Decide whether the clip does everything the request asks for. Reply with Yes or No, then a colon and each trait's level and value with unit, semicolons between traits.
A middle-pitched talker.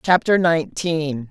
Yes: medium, 160 Hz